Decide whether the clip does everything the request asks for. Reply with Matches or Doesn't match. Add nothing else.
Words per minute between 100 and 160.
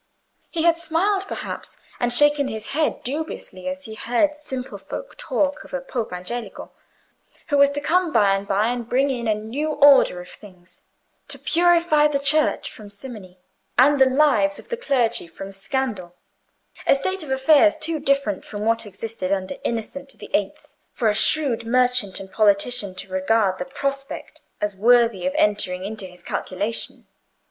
Doesn't match